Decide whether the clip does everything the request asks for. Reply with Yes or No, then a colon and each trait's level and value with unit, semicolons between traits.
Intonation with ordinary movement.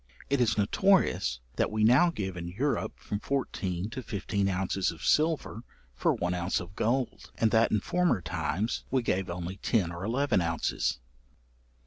No: wide, 5.8 semitones